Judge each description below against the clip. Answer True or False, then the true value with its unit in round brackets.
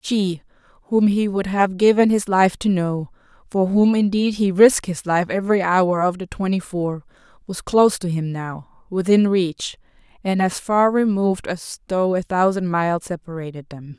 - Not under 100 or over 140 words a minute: False (170 wpm)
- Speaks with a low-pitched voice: False (185 Hz)